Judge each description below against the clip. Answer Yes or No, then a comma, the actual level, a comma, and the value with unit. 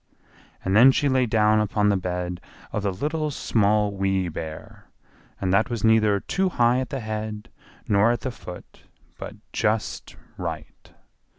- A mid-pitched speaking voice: No, low, 105 Hz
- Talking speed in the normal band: Yes, average, 160 wpm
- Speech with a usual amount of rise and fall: Yes, average, 3.4 semitones